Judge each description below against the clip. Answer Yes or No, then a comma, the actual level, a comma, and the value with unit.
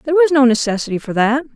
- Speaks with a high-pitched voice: Yes, very high, 255 Hz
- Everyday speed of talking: No, fast, 230 wpm